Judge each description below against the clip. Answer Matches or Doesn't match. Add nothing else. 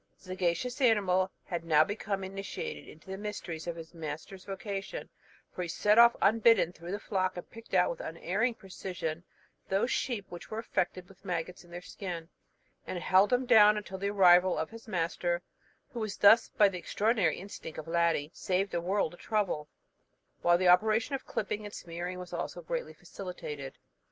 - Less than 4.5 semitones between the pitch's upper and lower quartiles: Matches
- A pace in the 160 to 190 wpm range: Matches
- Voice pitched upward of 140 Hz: Matches